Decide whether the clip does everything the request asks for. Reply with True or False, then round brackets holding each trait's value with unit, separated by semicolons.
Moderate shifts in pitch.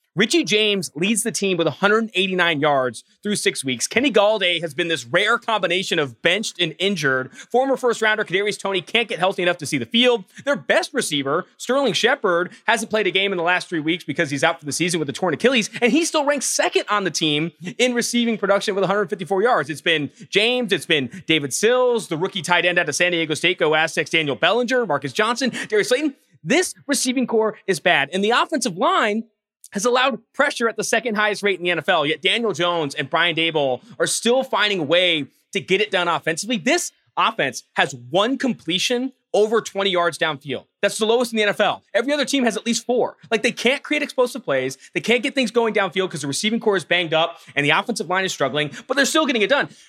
False (5.9 semitones)